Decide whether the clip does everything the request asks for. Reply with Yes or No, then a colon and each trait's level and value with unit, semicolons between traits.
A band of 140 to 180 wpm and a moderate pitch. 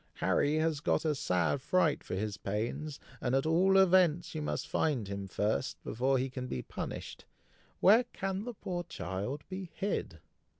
Yes: average, 170 wpm; medium, 150 Hz